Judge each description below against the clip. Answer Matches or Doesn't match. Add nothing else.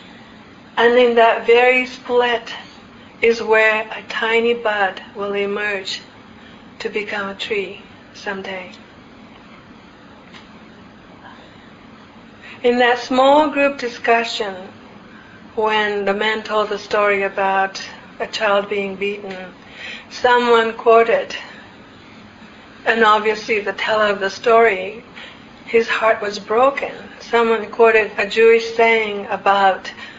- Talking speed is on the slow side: Matches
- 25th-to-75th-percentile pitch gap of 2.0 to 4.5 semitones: Matches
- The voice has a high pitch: Matches